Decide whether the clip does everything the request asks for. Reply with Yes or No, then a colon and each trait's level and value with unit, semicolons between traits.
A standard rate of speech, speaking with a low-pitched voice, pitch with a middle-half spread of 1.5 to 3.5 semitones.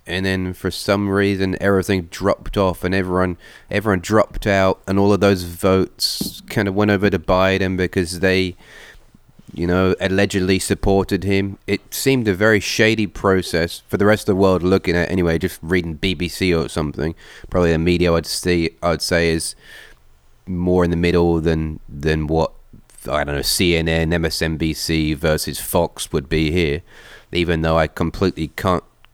Yes: average, 170 wpm; very low, 90 Hz; average, 3.0 semitones